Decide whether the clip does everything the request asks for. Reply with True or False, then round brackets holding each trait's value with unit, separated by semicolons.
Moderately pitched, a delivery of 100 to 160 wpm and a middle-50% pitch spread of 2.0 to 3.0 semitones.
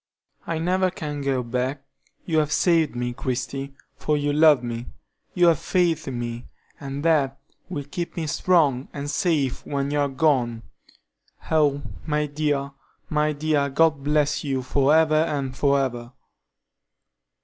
True (145 Hz; 150 wpm; 2.5 semitones)